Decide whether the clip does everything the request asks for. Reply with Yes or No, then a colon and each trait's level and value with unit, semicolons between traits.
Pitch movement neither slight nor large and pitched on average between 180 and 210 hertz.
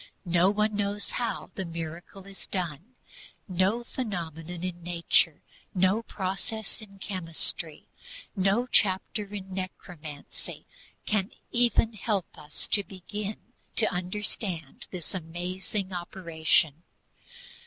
Yes: average, 3.3 semitones; medium, 185 Hz